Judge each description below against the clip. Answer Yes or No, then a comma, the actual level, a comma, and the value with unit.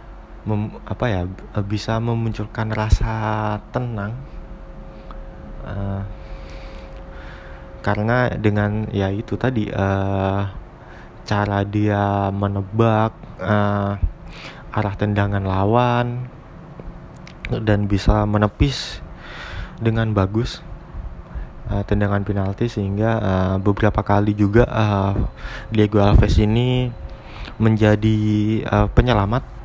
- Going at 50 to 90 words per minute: Yes, slow, 85 wpm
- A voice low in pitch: Yes, low, 105 Hz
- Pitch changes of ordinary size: No, narrow, 2.1 semitones